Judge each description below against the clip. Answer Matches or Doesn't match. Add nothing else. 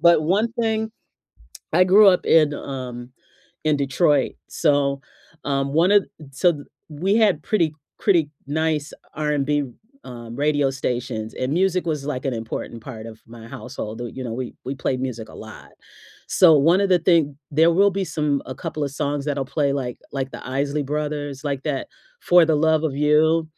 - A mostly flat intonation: Doesn't match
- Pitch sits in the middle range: Matches